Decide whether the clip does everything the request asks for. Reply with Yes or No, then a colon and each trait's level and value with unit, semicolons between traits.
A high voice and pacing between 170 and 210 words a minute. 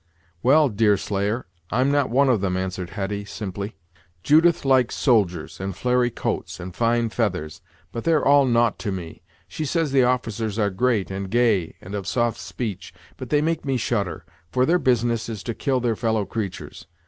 No: low, 115 Hz; average, 180 wpm